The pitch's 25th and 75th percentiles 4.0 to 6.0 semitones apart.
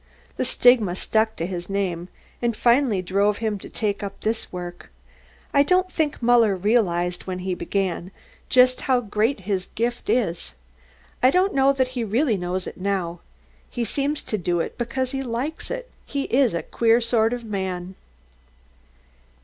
Yes: average, 5.2 semitones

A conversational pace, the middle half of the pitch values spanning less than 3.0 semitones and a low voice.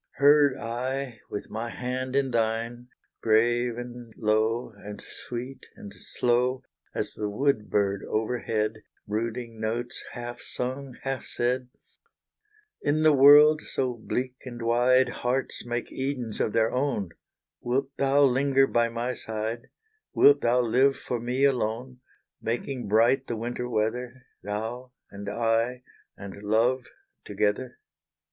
No: slow, 130 wpm; narrow, 2.5 semitones; low, 120 Hz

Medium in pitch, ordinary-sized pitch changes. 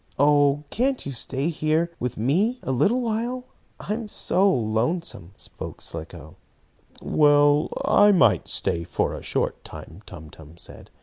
No: medium, 150 Hz; wide, 8.7 semitones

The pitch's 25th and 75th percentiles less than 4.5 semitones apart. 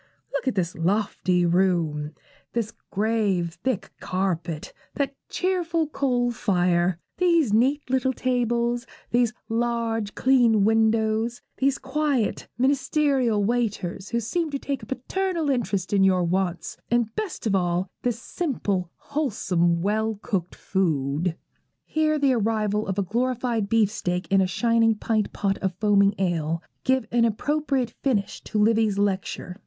No: average, 5.1 semitones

